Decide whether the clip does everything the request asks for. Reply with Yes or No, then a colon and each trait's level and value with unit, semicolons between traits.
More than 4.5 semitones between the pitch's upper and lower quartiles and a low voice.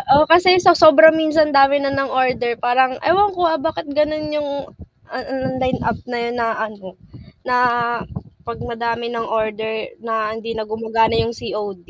No: average, 5.0 semitones; very high, 250 Hz